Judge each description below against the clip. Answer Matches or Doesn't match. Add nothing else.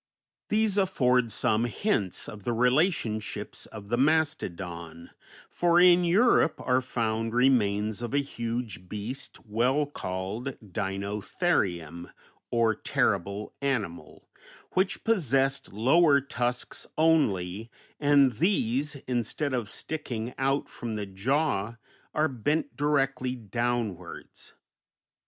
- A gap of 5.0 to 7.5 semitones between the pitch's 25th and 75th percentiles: Matches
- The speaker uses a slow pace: Matches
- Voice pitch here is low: Matches